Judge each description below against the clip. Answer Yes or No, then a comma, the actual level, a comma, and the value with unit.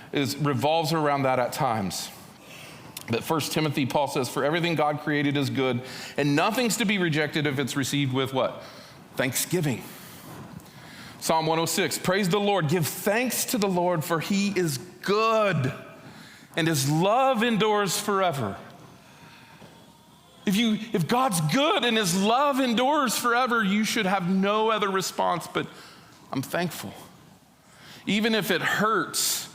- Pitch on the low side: No, medium, 180 Hz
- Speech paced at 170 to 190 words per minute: No, average, 140 wpm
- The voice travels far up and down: Yes, wide, 6.0 semitones